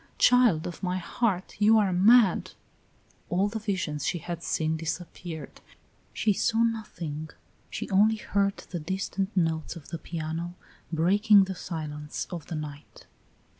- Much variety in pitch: No, average, 4.2 semitones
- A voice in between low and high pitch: Yes, medium, 180 Hz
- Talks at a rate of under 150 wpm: Yes, average, 140 wpm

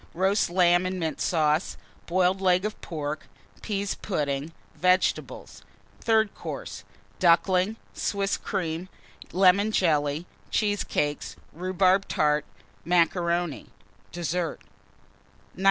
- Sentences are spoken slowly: Yes, slow, 95 wpm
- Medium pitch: Yes, medium, 180 Hz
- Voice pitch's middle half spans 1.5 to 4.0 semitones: Yes, average, 2.9 semitones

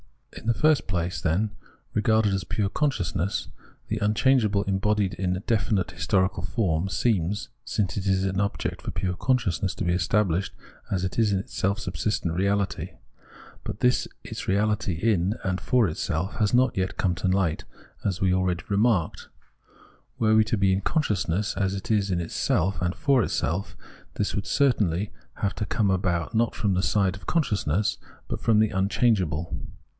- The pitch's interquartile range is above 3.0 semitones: No, average, 2.7 semitones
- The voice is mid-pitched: No, low, 100 Hz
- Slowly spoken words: No, average, 170 wpm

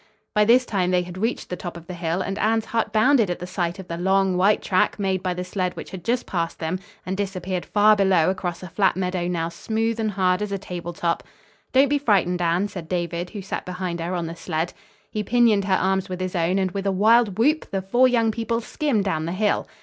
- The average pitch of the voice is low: No, high, 190 Hz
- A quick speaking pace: Yes, fast, 245 wpm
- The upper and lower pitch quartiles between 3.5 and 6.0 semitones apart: No, average, 3.0 semitones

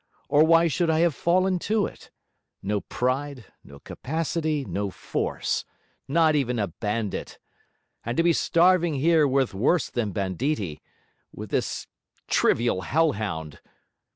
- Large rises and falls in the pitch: Yes, wide, 7.8 semitones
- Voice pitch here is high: No, medium, 140 Hz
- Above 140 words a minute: No, slow, 135 wpm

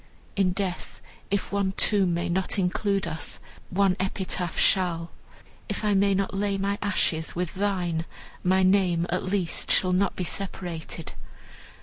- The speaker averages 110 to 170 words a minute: Yes, average, 145 wpm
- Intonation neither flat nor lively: No, narrow, 2.0 semitones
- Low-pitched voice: No, high, 190 Hz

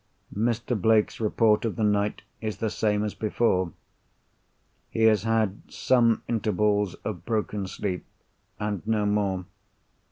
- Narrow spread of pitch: Yes, narrow, 1.5 semitones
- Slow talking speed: Yes, slow, 130 wpm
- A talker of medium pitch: No, low, 105 Hz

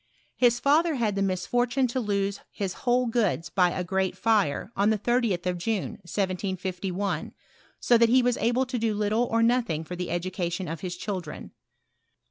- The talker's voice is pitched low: No, high, 205 Hz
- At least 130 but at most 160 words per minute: No, average, 175 wpm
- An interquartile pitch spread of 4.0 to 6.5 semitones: Yes, average, 4.6 semitones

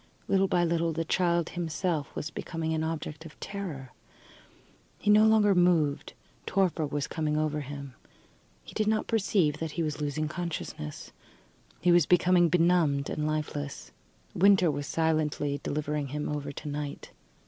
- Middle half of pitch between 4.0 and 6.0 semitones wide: No, average, 3.1 semitones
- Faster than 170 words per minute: No, average, 150 wpm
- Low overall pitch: No, medium, 160 Hz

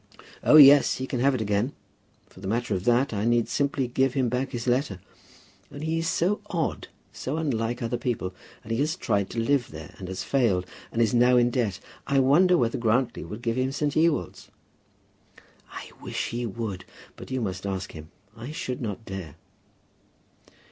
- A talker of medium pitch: No, low, 120 Hz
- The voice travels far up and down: No, average, 4.1 semitones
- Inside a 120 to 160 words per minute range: No, average, 190 wpm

